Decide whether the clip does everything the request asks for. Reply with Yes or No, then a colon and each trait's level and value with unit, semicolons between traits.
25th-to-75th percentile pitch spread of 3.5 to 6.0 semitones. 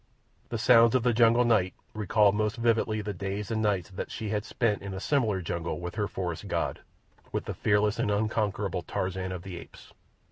No: average, 2.9 semitones